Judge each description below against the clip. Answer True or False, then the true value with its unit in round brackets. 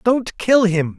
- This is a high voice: True (205 Hz)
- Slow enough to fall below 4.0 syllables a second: True (3.4 syllables/s)